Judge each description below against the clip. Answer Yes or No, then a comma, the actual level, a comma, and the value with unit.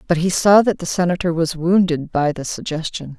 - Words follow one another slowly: No, fast, 205 wpm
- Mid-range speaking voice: Yes, medium, 170 Hz